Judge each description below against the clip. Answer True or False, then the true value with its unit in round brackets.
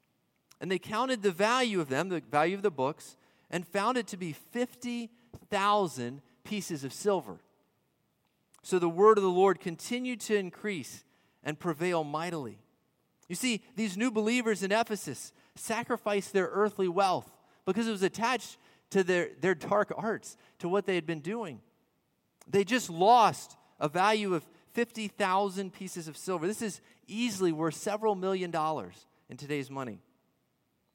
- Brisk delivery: False (155 wpm)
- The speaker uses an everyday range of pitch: True (4.4 semitones)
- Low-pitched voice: False (190 Hz)